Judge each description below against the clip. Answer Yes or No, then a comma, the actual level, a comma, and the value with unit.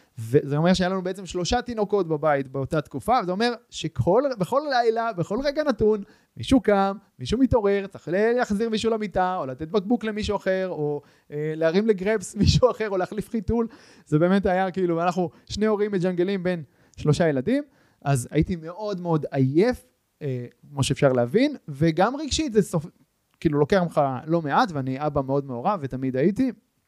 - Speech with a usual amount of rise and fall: No, wide, 6.4 semitones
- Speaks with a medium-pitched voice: Yes, medium, 180 Hz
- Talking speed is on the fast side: Yes, fast, 165 wpm